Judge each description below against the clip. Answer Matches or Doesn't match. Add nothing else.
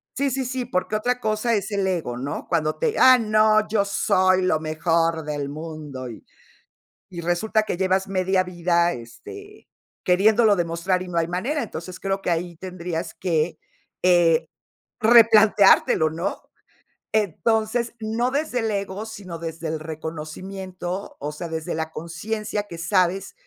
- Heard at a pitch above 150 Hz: Matches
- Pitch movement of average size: Matches